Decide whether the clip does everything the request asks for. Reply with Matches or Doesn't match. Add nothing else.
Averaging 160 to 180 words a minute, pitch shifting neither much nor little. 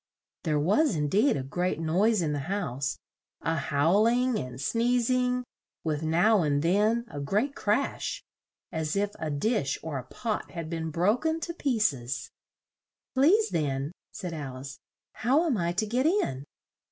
Doesn't match